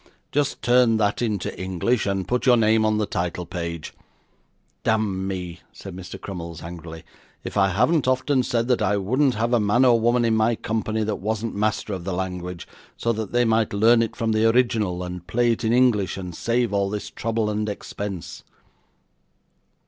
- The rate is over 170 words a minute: Yes, average, 185 wpm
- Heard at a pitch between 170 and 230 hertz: No, low, 110 Hz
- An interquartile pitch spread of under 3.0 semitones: No, average, 3.6 semitones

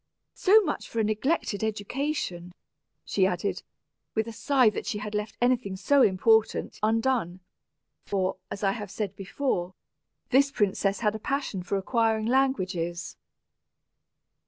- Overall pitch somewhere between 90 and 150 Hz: No, high, 215 Hz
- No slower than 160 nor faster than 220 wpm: No, slow, 135 wpm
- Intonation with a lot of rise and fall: No, average, 4.6 semitones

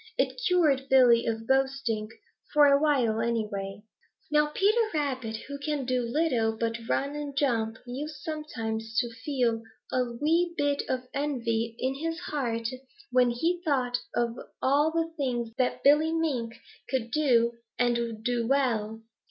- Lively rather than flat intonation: No, average, 4.2 semitones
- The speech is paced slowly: No, average, 145 wpm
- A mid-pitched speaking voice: No, very high, 255 Hz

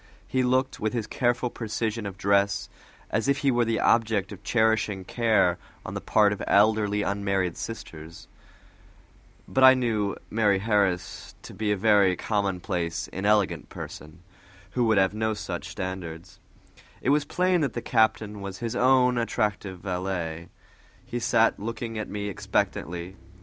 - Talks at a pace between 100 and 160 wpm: Yes, average, 155 wpm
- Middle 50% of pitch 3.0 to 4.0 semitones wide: Yes, average, 3.3 semitones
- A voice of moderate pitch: No, low, 105 Hz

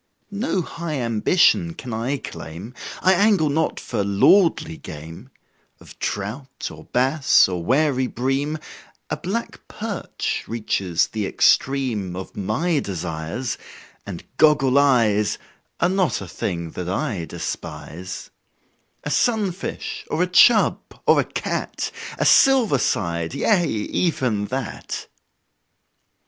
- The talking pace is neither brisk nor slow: No, slow, 120 wpm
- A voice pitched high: No, low, 130 Hz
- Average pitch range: No, wide, 9.0 semitones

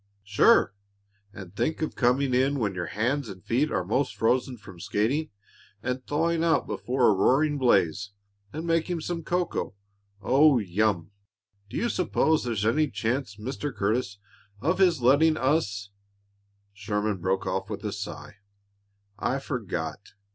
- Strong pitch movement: Yes, wide, 6.5 semitones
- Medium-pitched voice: No, low, 125 Hz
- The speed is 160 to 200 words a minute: No, average, 145 wpm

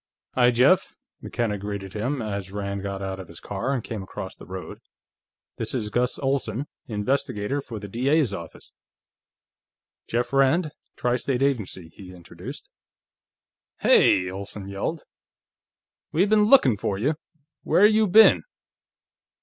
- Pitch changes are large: Yes, wide, 5.7 semitones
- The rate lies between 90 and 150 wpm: Yes, slow, 135 wpm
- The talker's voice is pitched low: Yes, low, 110 Hz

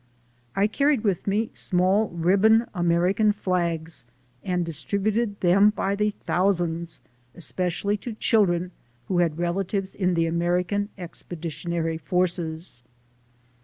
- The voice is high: No, medium, 180 Hz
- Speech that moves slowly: Yes, slow, 115 wpm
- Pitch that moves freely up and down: No, average, 3.0 semitones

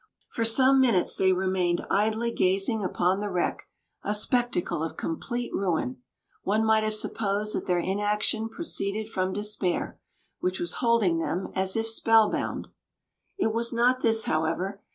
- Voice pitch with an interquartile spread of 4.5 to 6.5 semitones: No, average, 3.3 semitones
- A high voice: Yes, high, 210 Hz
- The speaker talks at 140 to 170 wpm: Yes, average, 150 wpm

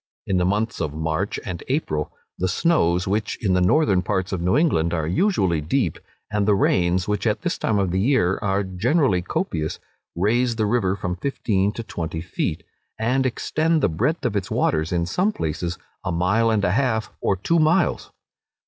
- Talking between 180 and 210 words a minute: Yes, average, 190 wpm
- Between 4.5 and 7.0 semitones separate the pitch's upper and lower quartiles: Yes, average, 5.0 semitones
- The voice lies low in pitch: Yes, very low, 95 Hz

